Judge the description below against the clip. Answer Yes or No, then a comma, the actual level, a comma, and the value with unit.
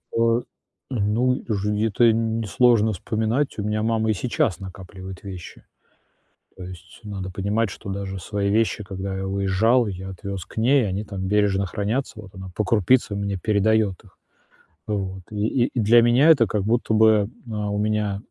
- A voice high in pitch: No, low, 105 Hz